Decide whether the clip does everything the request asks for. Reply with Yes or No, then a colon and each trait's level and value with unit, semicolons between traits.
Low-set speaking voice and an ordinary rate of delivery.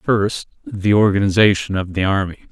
Yes: low, 100 Hz; average, 145 wpm